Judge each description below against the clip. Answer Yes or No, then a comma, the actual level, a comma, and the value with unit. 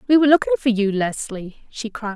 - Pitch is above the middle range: Yes, high, 220 Hz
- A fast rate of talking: Yes, fast, 225 wpm